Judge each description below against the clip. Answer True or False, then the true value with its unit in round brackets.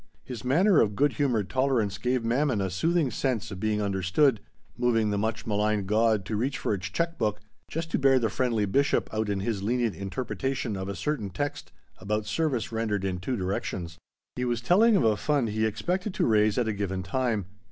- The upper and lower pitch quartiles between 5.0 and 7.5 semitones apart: False (4.3 semitones)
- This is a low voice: True (110 Hz)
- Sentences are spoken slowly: False (205 wpm)